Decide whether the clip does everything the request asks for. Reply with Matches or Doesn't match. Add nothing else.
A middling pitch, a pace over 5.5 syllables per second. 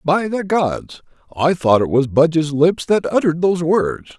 Doesn't match